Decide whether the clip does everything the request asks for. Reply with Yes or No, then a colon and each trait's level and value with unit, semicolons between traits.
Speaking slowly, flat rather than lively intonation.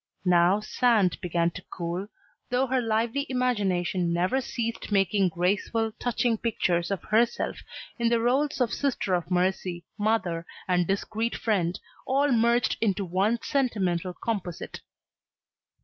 No: slow, 130 wpm; average, 4.8 semitones